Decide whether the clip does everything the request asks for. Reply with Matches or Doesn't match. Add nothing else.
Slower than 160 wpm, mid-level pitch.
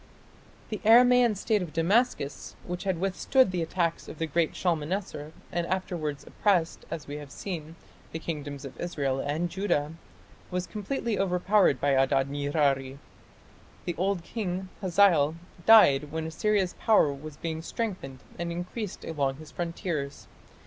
Matches